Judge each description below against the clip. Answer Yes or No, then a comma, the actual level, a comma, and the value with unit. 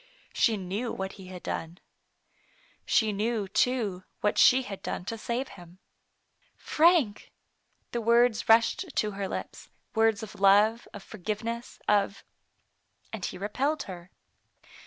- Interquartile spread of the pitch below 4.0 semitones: Yes, average, 3.2 semitones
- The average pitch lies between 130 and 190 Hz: No, high, 215 Hz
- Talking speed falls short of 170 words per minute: Yes, average, 145 wpm